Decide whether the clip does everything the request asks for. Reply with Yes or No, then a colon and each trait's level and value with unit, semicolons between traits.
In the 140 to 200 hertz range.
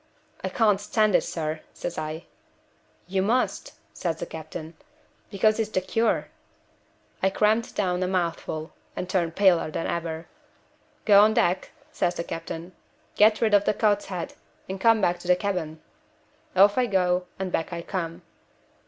Yes: medium, 185 Hz